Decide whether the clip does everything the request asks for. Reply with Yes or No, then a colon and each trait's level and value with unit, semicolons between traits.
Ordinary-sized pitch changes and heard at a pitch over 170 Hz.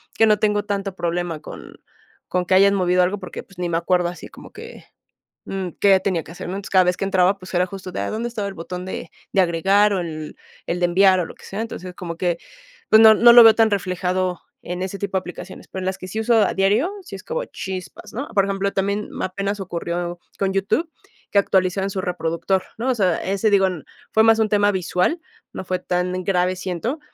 No: narrow, 2.2 semitones; high, 190 Hz